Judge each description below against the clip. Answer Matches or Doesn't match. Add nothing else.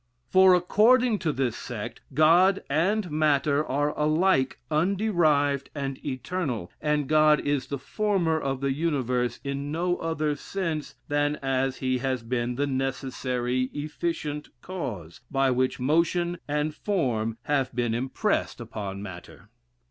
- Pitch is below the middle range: Doesn't match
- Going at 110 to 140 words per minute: Matches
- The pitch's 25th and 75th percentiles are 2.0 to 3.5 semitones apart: Doesn't match